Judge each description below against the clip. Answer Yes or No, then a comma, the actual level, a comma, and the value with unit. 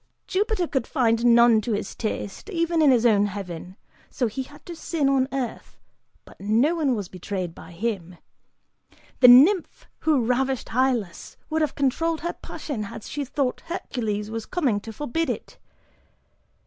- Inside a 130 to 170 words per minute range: Yes, average, 160 wpm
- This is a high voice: Yes, very high, 250 Hz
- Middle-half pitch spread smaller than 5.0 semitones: No, wide, 5.6 semitones